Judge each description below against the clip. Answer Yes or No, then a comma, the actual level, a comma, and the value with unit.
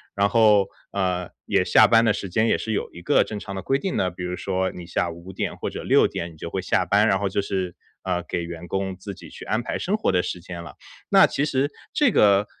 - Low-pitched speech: Yes, very low, 95 Hz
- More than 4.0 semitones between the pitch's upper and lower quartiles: No, average, 3.0 semitones